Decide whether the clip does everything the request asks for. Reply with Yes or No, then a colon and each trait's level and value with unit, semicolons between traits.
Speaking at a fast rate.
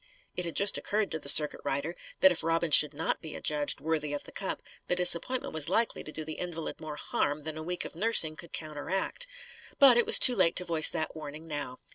Yes: fast, 230 wpm